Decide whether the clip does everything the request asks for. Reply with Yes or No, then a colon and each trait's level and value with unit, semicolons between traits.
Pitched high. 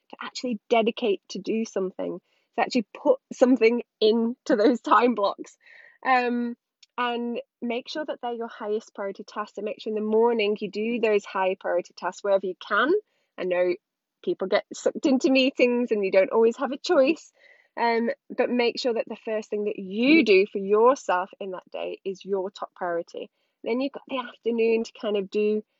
Yes: high, 230 Hz